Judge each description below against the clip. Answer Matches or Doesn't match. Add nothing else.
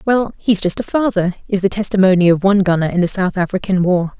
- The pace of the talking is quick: Matches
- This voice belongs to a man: Doesn't match